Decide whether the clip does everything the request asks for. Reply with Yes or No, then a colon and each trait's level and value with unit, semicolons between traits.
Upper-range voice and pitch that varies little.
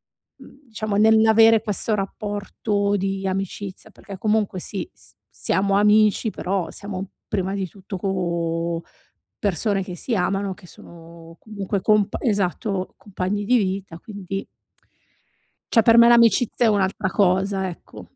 Yes: high, 200 Hz; narrow, 2.2 semitones